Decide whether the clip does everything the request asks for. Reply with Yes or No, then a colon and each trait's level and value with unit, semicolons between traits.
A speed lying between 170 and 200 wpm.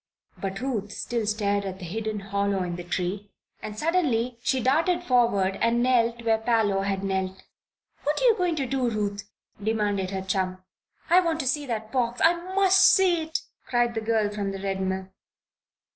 Yes: average, 185 wpm